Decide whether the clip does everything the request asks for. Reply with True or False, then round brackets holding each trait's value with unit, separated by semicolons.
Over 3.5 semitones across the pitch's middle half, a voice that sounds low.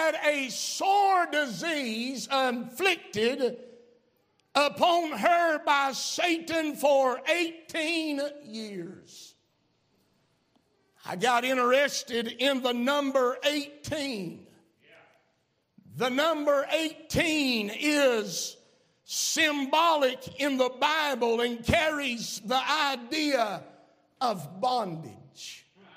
False (4.1 semitones; 275 Hz)